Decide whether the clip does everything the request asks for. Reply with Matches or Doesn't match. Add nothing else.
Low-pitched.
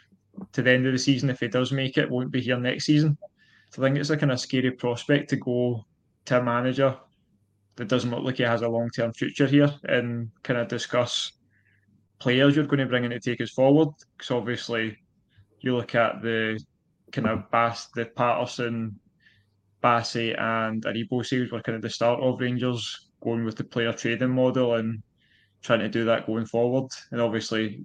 Matches